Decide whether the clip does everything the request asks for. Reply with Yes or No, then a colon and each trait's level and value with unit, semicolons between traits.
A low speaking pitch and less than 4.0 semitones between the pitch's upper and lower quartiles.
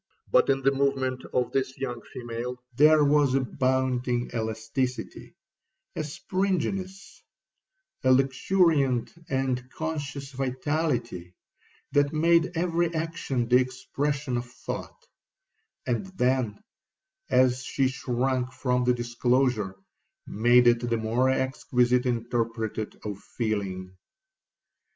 Yes: low, 130 Hz; narrow, 2.5 semitones